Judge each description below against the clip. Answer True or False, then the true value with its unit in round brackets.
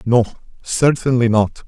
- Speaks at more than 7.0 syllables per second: False (4.2 syllables/s)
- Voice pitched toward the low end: True (120 Hz)